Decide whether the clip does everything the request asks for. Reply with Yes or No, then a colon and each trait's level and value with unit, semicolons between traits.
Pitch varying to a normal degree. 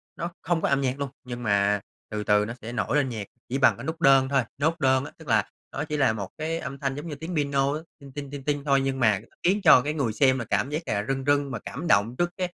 Yes: average, 3.6 semitones